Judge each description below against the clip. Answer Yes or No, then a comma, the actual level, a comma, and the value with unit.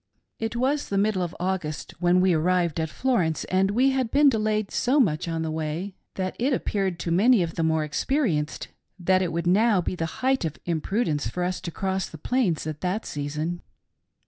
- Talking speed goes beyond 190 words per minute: Yes, average, 200 wpm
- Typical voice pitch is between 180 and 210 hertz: Yes, medium, 185 Hz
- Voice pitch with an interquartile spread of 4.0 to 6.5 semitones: Yes, average, 4.9 semitones